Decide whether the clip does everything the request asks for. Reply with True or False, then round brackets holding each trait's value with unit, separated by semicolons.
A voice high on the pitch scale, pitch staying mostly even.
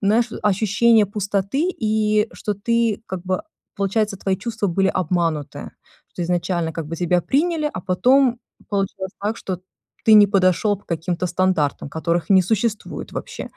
False (195 Hz; 3.3 semitones)